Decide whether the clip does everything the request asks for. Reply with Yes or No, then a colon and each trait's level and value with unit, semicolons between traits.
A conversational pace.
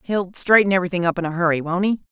No: fast, 255 wpm